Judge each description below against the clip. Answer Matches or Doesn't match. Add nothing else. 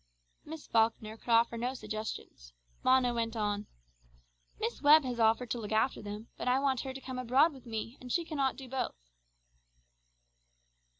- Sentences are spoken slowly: Doesn't match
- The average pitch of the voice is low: Doesn't match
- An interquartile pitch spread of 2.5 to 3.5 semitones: Matches